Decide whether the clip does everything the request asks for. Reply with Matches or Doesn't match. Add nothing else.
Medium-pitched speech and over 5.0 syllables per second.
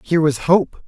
Matches